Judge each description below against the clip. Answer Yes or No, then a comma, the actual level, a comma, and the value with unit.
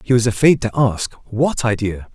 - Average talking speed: Yes, average, 195 wpm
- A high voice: No, low, 115 Hz